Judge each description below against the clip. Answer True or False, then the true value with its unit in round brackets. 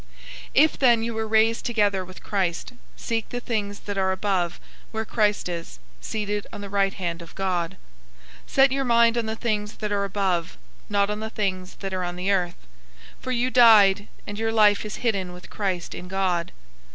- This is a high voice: True (205 Hz)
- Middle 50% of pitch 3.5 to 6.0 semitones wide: False (3.1 semitones)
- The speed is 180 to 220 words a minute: True (200 wpm)